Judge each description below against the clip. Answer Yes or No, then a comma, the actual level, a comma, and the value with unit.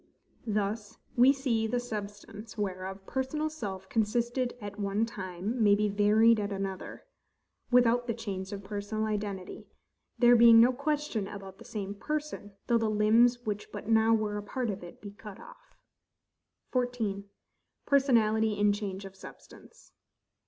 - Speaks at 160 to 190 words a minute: No, average, 150 wpm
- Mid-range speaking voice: No, high, 215 Hz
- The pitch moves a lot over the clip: No, average, 3.1 semitones